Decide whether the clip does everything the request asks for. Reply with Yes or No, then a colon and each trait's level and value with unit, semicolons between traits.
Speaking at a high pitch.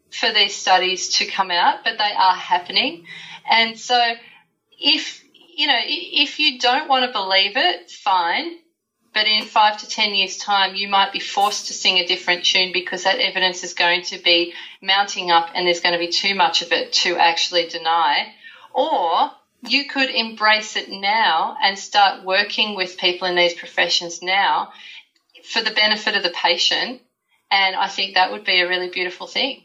Yes: high, 200 Hz